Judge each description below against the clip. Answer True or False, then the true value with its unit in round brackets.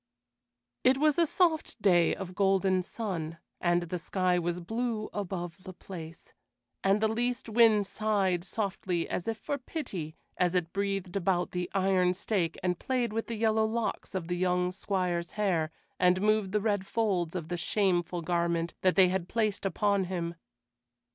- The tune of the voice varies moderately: True (3.4 semitones)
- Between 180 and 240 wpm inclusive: False (165 wpm)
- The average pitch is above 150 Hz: True (190 Hz)